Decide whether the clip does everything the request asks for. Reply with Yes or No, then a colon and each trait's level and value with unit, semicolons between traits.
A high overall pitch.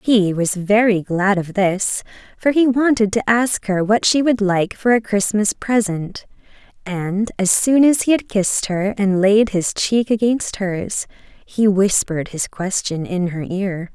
Yes: high, 205 Hz